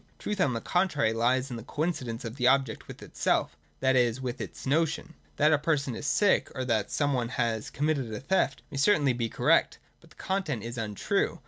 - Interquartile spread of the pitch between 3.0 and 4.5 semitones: Yes, average, 4.1 semitones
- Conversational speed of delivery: No, fast, 215 wpm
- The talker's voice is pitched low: Yes, low, 130 Hz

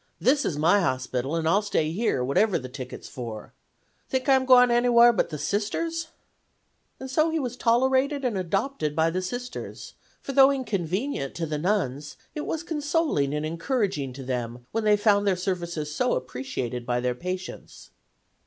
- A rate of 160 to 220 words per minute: Yes, average, 170 wpm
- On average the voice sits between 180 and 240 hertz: Yes, high, 190 Hz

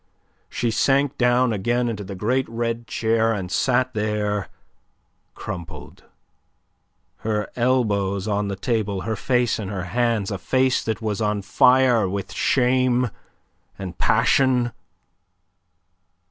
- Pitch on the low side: Yes, low, 115 Hz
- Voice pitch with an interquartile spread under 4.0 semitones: Yes, average, 3.4 semitones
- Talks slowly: Yes, slow, 120 wpm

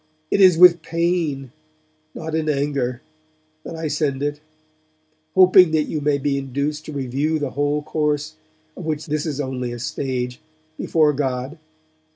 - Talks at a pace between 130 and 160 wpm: Yes, average, 155 wpm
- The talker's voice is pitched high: No, medium, 150 Hz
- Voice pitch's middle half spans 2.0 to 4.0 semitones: Yes, narrow, 2.6 semitones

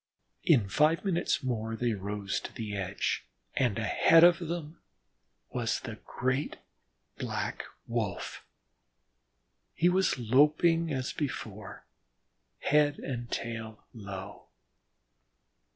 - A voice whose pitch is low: Yes, low, 125 Hz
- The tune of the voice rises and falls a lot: Yes, wide, 6.2 semitones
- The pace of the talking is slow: Yes, slow, 105 wpm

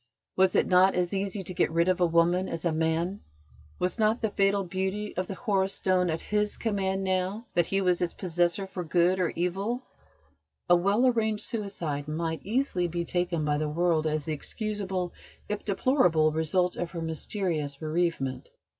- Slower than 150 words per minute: No, average, 180 wpm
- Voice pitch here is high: No, medium, 180 Hz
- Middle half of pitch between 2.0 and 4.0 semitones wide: Yes, average, 2.9 semitones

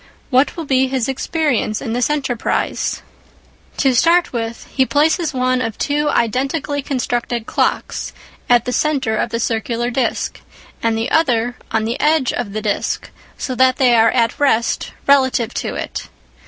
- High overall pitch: Yes, very high, 255 Hz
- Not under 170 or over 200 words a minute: No, average, 160 wpm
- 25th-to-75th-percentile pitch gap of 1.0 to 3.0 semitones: No, average, 3.4 semitones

